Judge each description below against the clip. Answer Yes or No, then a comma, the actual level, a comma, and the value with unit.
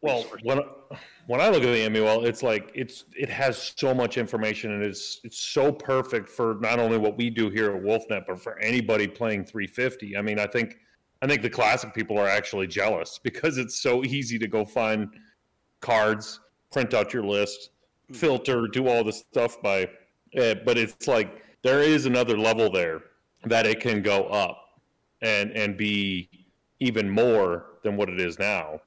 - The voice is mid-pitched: No, low, 110 Hz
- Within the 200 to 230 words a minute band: No, average, 185 wpm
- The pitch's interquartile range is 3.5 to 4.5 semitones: No, narrow, 2.5 semitones